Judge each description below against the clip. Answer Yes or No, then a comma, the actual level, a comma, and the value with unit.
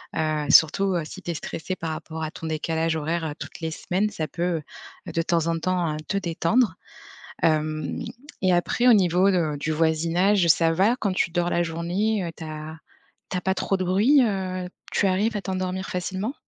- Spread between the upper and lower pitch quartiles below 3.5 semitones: Yes, average, 2.8 semitones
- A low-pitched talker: No, medium, 175 Hz